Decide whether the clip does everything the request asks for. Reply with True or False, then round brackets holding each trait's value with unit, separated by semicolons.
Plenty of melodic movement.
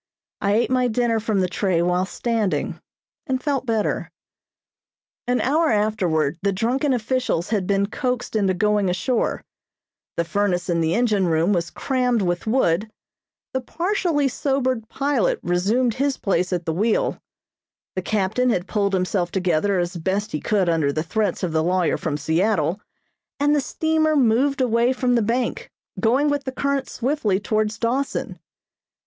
True (5.8 semitones)